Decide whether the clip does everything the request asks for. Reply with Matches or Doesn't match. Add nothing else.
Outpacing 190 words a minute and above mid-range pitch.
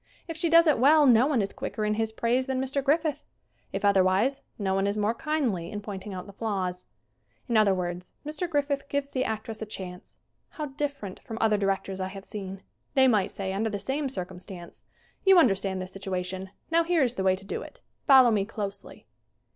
Matches